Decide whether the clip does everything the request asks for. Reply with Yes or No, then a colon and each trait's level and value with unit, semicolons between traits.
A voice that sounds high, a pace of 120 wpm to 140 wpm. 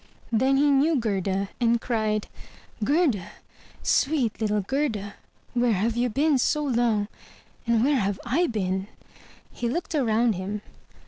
Yes: high, 235 Hz; slow, 135 wpm